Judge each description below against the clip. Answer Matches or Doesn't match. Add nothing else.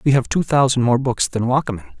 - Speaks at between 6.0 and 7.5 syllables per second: Matches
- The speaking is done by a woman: Doesn't match